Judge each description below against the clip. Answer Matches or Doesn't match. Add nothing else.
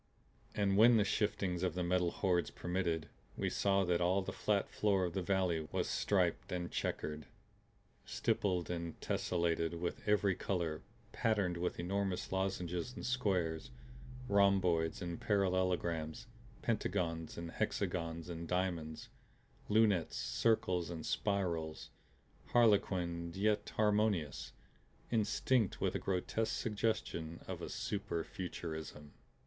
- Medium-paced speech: Doesn't match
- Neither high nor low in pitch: Doesn't match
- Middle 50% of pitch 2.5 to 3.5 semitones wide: Matches